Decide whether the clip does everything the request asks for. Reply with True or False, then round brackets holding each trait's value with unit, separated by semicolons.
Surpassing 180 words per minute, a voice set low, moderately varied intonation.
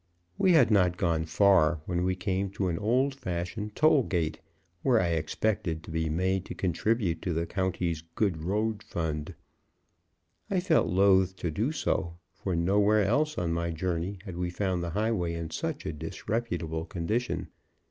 False (170 wpm; 90 Hz; 4.0 semitones)